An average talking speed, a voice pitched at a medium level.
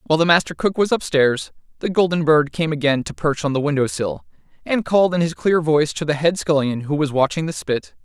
No: fast, 240 wpm; medium, 155 Hz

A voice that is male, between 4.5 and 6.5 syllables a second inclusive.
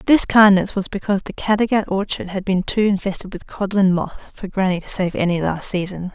No: female; 5.6 syllables/s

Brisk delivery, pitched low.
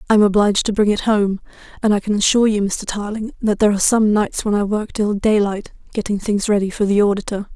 No: fast, 240 wpm; high, 205 Hz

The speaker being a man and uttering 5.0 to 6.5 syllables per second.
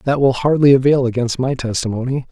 Yes: male; 5.8 syllables/s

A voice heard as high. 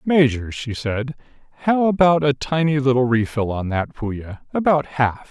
No: low, 135 Hz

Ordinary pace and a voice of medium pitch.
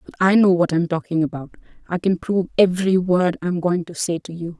No: fast, 220 wpm; medium, 175 Hz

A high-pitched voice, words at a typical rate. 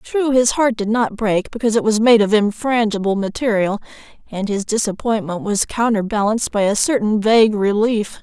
Yes: high, 215 Hz; average, 175 wpm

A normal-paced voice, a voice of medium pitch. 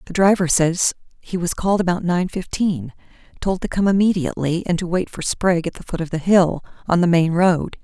No: fast, 215 wpm; medium, 175 Hz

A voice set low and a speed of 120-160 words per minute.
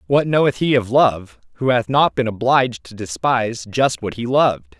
No: low, 120 Hz; average, 200 wpm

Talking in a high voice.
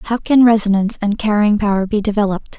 Yes: high, 210 Hz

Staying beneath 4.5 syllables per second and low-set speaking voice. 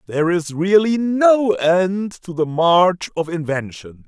No: 3.7 syllables/s; medium, 180 Hz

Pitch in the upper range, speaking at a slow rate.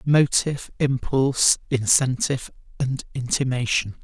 No: low, 135 Hz; slow, 75 wpm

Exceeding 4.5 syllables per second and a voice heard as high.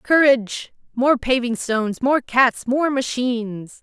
No: 3.9 syllables/s; very high, 250 Hz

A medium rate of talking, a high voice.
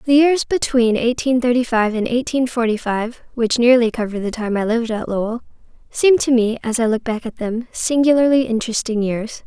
Yes: average, 195 wpm; high, 235 Hz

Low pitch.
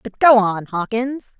No: high, 220 Hz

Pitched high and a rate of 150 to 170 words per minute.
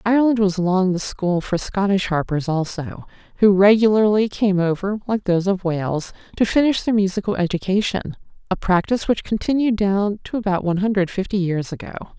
Yes: high, 195 Hz; average, 160 wpm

